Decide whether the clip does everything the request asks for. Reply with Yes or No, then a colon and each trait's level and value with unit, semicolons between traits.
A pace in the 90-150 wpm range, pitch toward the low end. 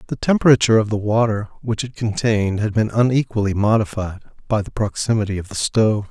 No: average, 175 wpm; low, 110 Hz